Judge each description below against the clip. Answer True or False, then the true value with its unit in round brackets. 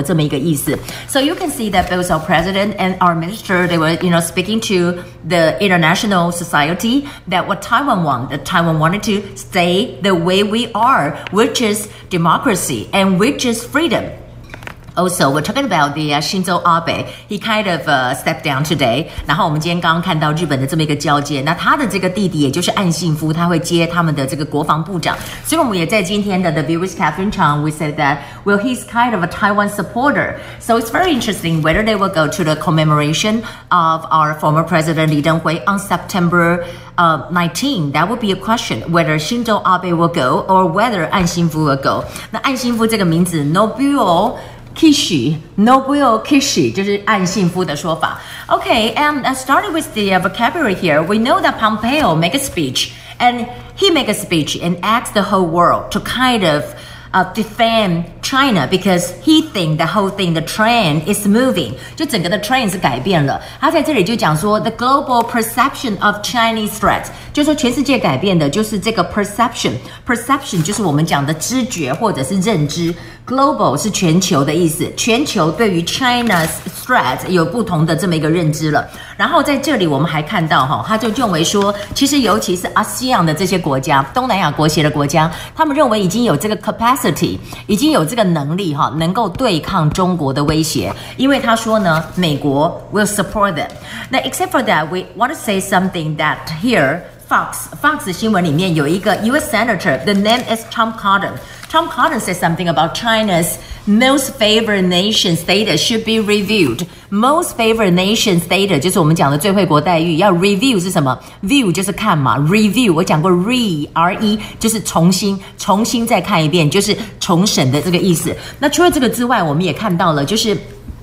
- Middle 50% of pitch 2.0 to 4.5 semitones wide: False (5.5 semitones)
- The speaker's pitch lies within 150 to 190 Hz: True (185 Hz)